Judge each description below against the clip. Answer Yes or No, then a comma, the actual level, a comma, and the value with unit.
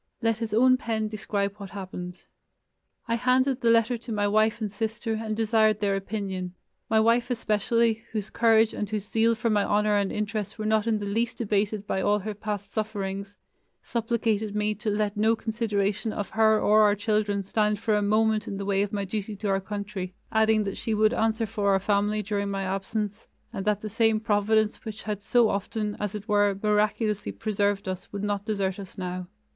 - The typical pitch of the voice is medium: No, high, 210 Hz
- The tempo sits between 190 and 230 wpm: Yes, average, 200 wpm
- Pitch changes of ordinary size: No, narrow, 1.5 semitones